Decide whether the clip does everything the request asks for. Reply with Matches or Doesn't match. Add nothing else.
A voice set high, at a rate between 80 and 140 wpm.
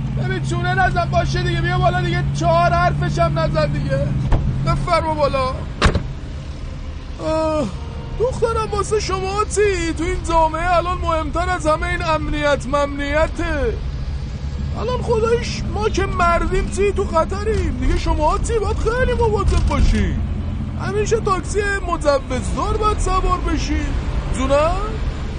Matches